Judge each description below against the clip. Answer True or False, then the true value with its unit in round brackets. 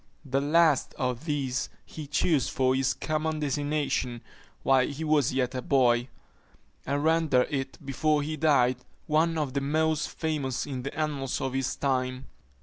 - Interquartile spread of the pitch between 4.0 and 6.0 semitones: False (2.9 semitones)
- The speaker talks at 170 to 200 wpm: False (155 wpm)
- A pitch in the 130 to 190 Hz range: True (140 Hz)